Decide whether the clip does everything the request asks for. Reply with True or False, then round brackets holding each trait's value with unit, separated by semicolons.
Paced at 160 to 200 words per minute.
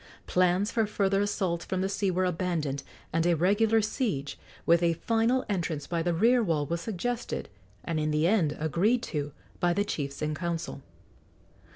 True (175 wpm)